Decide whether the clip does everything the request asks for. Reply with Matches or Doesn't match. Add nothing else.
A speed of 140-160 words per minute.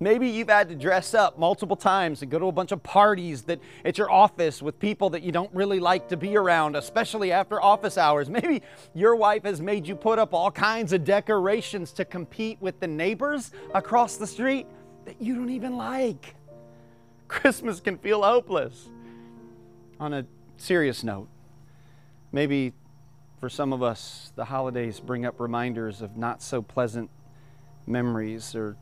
Doesn't match